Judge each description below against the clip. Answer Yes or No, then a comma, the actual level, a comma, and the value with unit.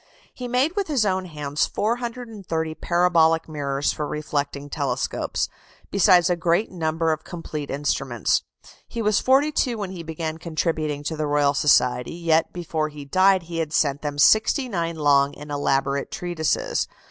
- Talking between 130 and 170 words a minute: Yes, average, 160 wpm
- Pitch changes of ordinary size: Yes, average, 4.2 semitones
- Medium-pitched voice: Yes, medium, 160 Hz